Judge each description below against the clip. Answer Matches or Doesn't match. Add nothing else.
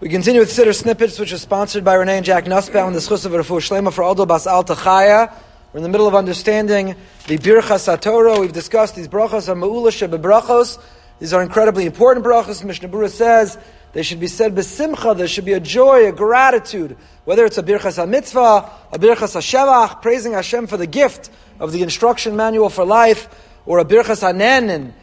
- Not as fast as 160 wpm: Doesn't match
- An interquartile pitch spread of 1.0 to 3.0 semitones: Doesn't match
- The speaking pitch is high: Matches